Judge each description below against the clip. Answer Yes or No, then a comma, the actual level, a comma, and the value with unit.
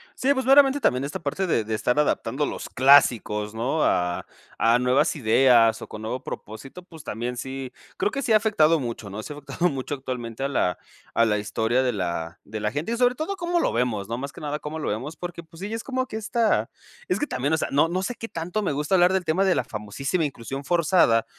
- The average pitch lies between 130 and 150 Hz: Yes, medium, 140 Hz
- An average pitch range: No, wide, 7.6 semitones